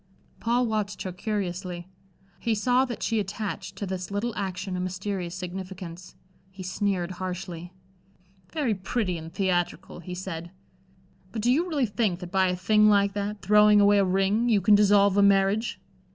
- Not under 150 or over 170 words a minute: Yes, average, 165 wpm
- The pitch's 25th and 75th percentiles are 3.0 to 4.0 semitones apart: No, narrow, 2.5 semitones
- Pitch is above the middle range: Yes, high, 195 Hz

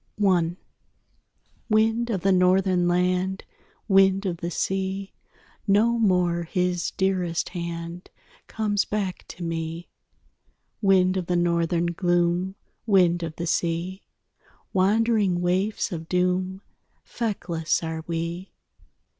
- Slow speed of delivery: Yes, slow, 115 wpm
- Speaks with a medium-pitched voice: Yes, medium, 180 Hz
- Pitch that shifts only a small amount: Yes, narrow, 2.1 semitones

